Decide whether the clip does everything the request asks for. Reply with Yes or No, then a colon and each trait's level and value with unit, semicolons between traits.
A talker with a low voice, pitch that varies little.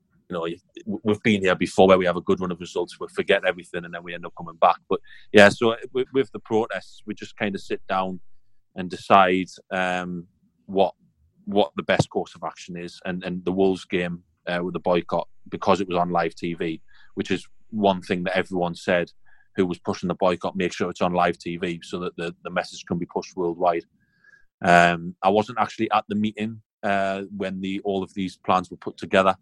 Yes: very low, 95 Hz; narrow, 2.2 semitones